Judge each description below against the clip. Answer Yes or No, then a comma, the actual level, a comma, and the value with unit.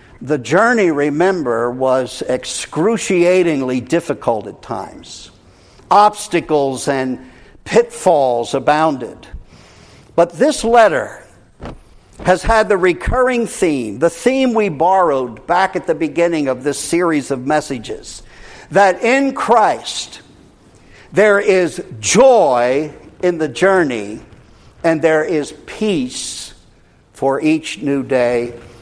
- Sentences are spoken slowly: Yes, slow, 105 wpm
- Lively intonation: Yes, wide, 6.4 semitones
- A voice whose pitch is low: No, medium, 155 Hz